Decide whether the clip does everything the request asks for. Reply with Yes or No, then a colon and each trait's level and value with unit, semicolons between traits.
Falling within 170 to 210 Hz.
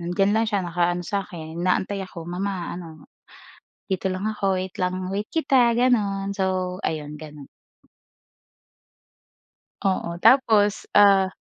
Yes: high, 190 Hz